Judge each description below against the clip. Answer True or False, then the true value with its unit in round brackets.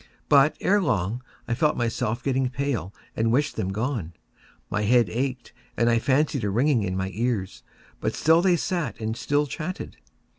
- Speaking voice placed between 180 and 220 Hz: False (120 Hz)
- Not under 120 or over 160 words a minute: False (175 wpm)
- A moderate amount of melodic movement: True (4.9 semitones)